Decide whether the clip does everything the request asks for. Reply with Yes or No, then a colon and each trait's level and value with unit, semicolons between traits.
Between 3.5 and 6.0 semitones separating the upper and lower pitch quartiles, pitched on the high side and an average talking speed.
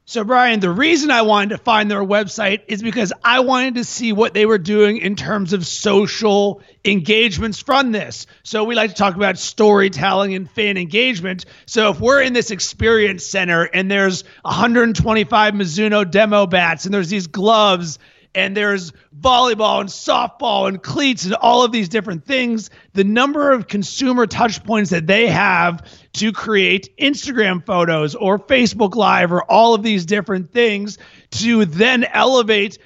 No: average, 2.8 semitones; high, 210 Hz; average, 170 wpm